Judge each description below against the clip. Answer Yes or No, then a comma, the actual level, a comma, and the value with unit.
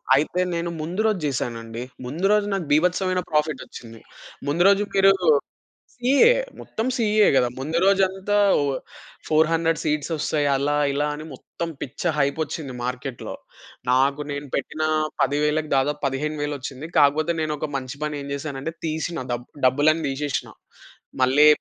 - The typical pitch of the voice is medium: Yes, medium, 150 Hz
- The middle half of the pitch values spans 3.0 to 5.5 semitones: Yes, average, 3.4 semitones